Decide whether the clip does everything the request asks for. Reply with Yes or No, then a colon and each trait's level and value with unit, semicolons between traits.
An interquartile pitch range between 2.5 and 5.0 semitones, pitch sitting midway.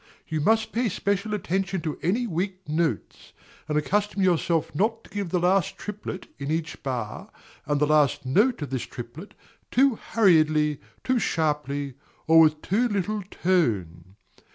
No: wide, 5.4 semitones; medium, 170 Hz